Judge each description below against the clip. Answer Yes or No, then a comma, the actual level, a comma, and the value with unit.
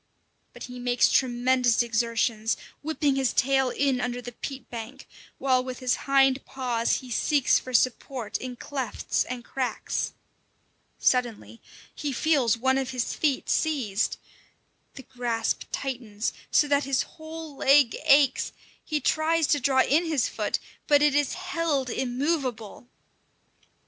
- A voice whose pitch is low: No, very high, 260 Hz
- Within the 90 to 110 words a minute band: No, average, 140 wpm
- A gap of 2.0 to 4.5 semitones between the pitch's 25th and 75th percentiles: Yes, average, 2.7 semitones